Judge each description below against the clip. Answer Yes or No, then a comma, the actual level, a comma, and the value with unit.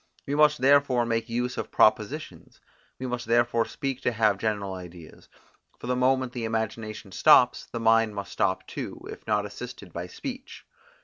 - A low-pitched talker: Yes, low, 115 Hz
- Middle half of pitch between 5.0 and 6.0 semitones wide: No, average, 3.1 semitones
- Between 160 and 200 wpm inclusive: Yes, average, 170 wpm